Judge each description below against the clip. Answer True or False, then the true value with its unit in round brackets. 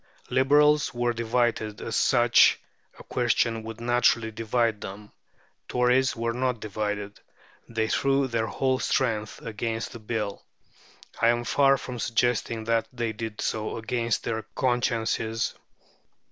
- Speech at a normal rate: False (130 wpm)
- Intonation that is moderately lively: False (1.8 semitones)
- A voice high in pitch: False (115 Hz)